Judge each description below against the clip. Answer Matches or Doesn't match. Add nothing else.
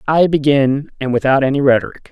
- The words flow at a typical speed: Matches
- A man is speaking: Matches